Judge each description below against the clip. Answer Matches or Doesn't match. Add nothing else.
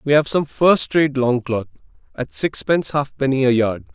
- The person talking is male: Matches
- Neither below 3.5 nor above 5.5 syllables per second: Matches